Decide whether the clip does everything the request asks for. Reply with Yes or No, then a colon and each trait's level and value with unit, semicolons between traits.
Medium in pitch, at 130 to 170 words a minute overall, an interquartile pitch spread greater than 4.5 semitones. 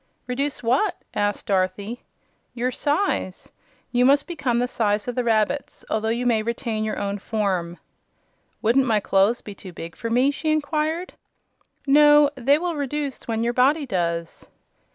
No: high, 240 Hz; average, 155 wpm; average, 5.2 semitones